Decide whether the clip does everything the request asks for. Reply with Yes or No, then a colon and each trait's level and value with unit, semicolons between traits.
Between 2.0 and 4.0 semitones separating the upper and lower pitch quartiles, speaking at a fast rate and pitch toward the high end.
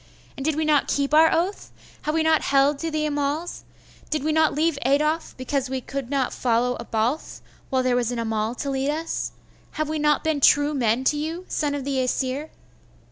Yes: average, 3.0 semitones; fast, 210 wpm; very high, 285 Hz